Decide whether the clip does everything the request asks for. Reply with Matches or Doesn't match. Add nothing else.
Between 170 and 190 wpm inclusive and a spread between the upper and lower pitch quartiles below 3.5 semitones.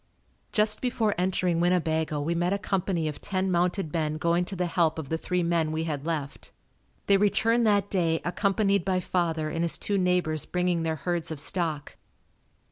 Matches